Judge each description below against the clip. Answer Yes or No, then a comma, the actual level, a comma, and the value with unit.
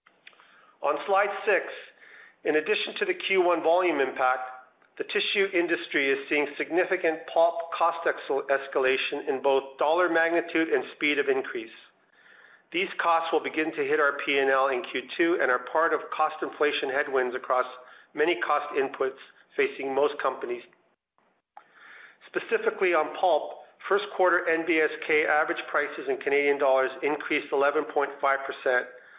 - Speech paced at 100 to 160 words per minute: Yes, slow, 135 wpm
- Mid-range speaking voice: Yes, medium, 165 Hz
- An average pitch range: No, wide, 6.3 semitones